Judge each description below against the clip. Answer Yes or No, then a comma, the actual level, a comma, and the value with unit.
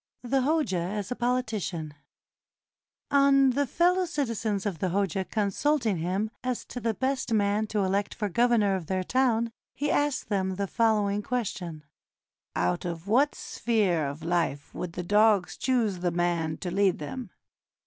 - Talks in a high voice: Yes, high, 205 Hz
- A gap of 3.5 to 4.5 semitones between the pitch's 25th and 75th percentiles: No, wide, 5.5 semitones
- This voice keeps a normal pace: Yes, average, 160 wpm